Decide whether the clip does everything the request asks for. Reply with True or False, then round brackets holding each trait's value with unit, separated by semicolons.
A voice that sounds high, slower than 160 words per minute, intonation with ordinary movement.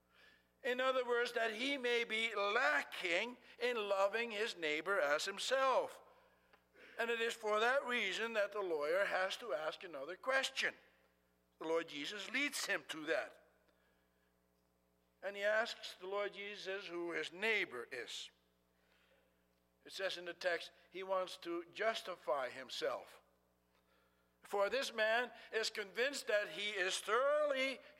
False (200 Hz; 135 wpm; 7.1 semitones)